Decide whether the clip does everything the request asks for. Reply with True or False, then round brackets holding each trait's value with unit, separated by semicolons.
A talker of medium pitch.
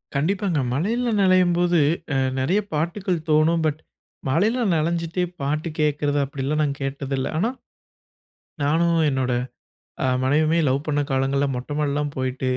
True (155 Hz)